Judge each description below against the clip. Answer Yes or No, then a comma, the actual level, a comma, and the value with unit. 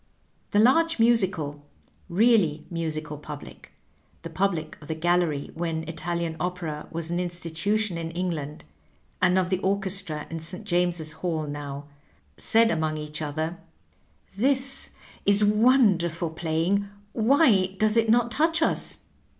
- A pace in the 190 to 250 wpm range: No, average, 140 wpm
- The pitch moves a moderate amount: Yes, average, 4.6 semitones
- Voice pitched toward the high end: No, medium, 175 Hz